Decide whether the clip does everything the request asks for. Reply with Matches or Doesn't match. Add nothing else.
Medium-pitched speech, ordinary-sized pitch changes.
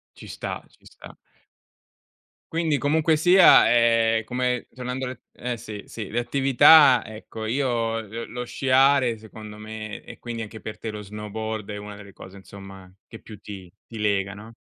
Doesn't match